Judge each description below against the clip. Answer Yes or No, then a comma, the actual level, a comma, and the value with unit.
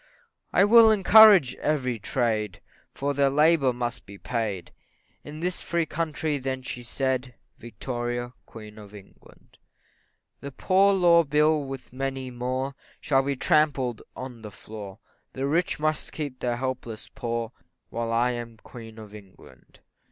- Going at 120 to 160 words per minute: Yes, average, 145 wpm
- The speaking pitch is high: No, low, 130 Hz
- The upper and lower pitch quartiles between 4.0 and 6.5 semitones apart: Yes, average, 4.4 semitones